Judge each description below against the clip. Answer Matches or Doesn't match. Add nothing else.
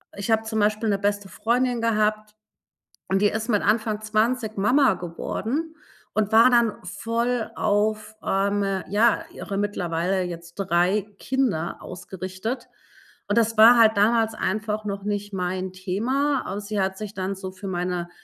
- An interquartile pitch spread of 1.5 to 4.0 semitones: Matches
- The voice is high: Matches